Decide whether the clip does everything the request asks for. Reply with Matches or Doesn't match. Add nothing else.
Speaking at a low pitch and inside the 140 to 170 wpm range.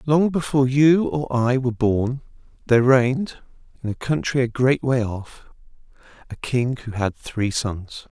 Matches